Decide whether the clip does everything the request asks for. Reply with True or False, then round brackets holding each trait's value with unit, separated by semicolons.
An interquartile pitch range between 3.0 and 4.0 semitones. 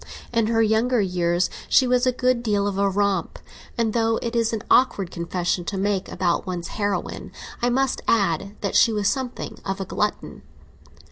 True (3.4 semitones)